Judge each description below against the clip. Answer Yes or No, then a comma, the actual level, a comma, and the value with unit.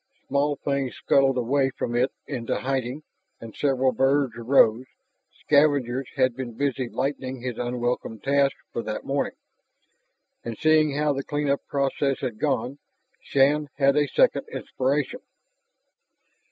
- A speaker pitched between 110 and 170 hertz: Yes, low, 135 Hz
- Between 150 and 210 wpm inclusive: No, slow, 135 wpm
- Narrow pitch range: Yes, narrow, 2.3 semitones